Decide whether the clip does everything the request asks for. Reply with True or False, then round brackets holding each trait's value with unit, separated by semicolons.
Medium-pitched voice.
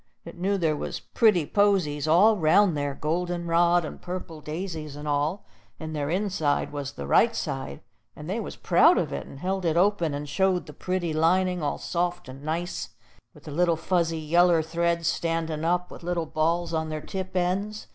True (170 Hz)